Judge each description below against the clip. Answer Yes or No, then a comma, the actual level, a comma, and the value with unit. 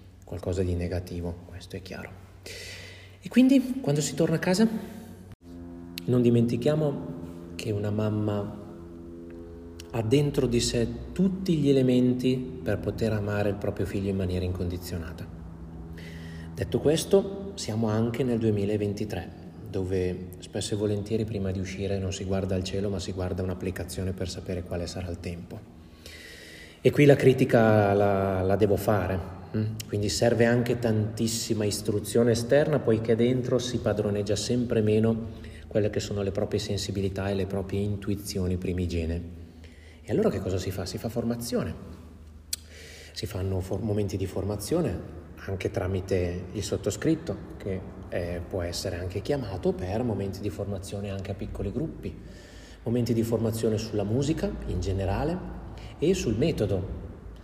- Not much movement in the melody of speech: No, average, 3.8 semitones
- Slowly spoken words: No, average, 140 wpm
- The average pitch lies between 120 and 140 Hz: No, low, 100 Hz